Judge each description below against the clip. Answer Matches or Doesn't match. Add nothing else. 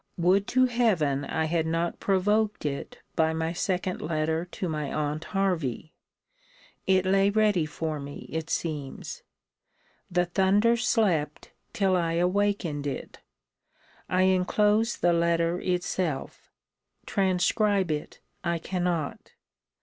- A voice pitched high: Doesn't match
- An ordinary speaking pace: Doesn't match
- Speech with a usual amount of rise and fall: Matches